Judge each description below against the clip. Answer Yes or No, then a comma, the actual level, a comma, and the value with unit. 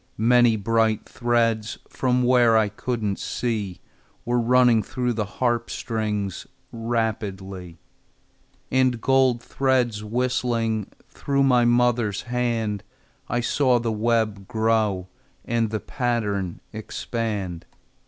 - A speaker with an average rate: No, slow, 105 wpm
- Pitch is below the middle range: Yes, low, 115 Hz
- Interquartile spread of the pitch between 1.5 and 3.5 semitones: Yes, narrow, 2.4 semitones